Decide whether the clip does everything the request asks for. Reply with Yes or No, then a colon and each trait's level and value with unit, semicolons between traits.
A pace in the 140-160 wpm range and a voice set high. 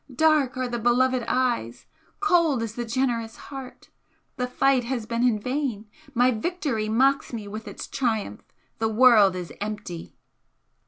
Yes: average, 150 wpm; high, 240 Hz